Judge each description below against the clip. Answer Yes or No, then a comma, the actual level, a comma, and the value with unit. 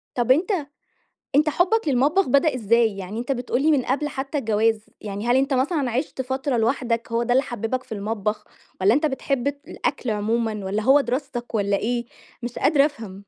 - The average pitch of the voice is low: No, high, 245 Hz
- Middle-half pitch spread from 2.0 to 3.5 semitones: No, average, 3.9 semitones